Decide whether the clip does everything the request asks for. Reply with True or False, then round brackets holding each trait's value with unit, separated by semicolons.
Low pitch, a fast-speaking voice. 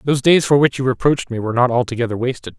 True (130 Hz; 255 wpm)